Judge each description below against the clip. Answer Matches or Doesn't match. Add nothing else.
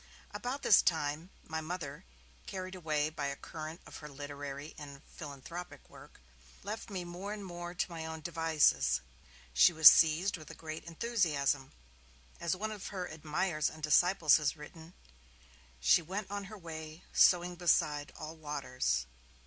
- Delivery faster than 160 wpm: Doesn't match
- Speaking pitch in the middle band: Matches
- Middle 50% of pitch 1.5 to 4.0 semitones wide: Matches